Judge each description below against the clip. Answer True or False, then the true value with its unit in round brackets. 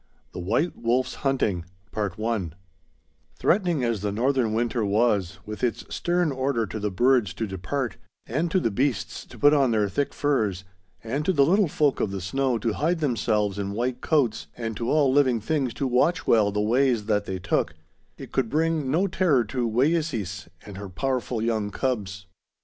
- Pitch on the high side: False (120 Hz)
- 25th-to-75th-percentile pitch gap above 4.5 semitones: True (5.1 semitones)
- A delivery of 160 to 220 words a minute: True (180 wpm)